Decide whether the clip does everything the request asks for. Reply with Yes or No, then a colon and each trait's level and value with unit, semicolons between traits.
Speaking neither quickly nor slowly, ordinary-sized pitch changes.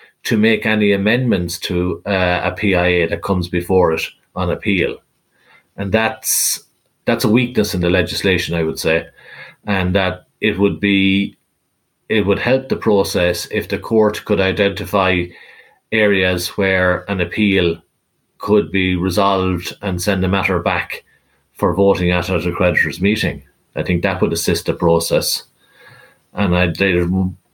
No: average, 145 wpm; narrow, 2.3 semitones